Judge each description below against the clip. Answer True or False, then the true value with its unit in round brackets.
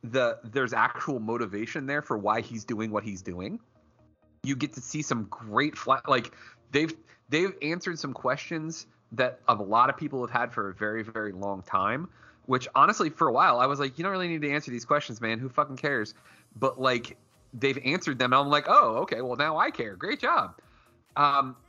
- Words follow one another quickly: True (210 wpm)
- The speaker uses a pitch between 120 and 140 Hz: True (125 Hz)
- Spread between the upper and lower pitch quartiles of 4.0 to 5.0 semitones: True (4.6 semitones)